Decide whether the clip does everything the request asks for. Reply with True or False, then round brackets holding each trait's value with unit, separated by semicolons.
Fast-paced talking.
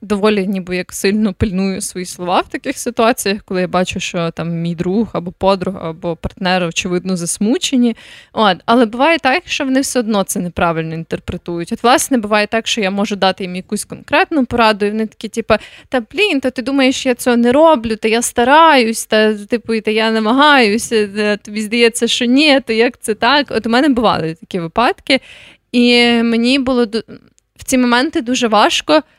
True (190 wpm)